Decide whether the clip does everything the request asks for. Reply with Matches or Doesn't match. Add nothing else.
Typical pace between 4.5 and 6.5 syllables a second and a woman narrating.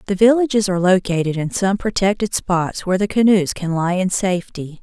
Matches